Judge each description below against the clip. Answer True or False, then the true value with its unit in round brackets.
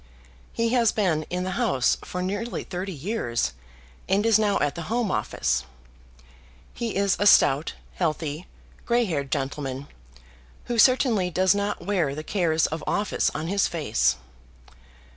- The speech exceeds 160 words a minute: False (145 wpm)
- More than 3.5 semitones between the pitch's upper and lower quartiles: True (5.3 semitones)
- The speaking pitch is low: False (185 Hz)